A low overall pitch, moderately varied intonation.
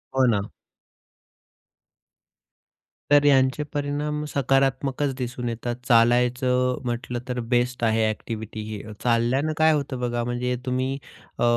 No: low, 125 Hz; narrow, 2.1 semitones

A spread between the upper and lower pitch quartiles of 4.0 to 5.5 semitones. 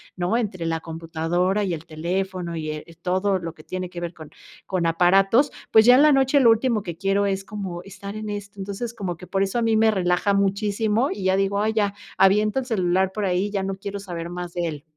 No: average, 2.9 semitones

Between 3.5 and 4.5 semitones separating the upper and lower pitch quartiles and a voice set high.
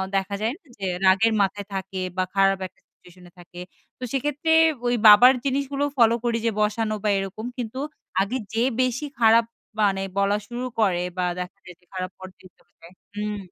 Yes: average, 3.9 semitones; high, 210 Hz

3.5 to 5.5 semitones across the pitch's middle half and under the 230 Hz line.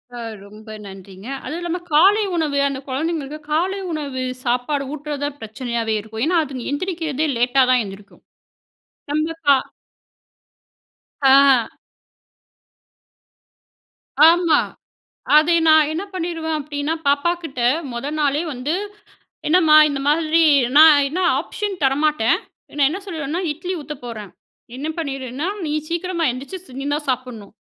No: average, 4.1 semitones; very high, 295 Hz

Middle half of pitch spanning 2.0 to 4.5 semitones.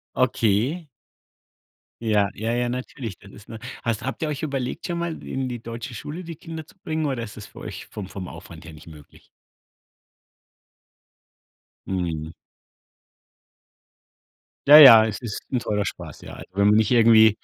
No: average, 5.0 semitones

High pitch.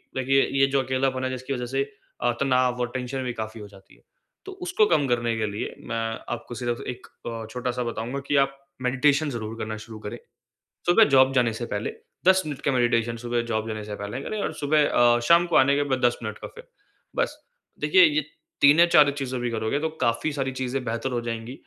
No: low, 125 Hz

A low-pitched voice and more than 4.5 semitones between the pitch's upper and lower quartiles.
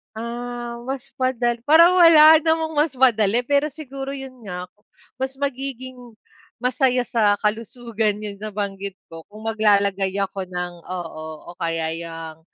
No: high, 235 Hz; average, 5.2 semitones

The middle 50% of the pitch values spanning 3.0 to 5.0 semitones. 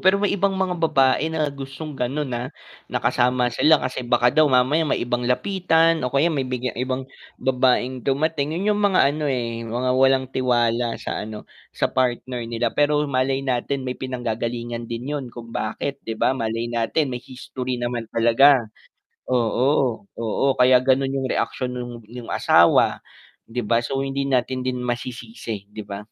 No: narrow, 2.6 semitones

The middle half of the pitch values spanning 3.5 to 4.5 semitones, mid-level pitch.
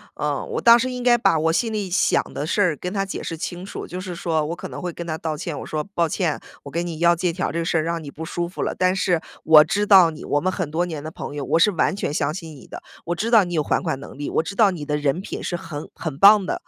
No: average, 3.1 semitones; medium, 170 Hz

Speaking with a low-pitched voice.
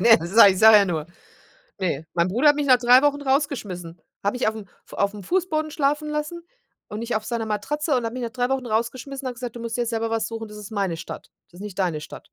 No: high, 230 Hz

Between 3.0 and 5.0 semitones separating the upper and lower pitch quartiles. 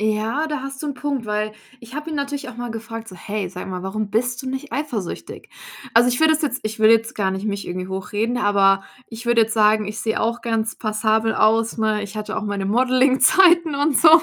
Yes: average, 3.5 semitones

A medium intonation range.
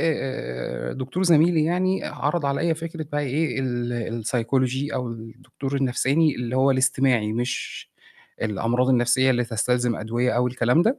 Yes: average, 3.4 semitones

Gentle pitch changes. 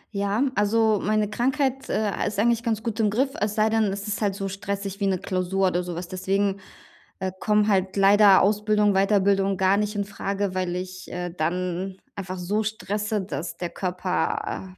Yes: narrow, 2.1 semitones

